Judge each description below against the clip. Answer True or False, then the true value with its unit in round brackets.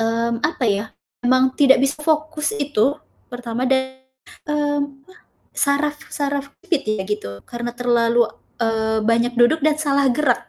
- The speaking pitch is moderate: False (260 Hz)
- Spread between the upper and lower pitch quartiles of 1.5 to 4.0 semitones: True (3.6 semitones)